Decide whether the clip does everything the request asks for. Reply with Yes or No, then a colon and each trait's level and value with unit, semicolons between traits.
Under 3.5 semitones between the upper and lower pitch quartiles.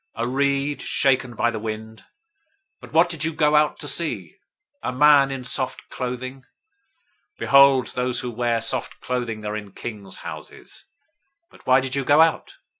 Yes: average, 3.0 semitones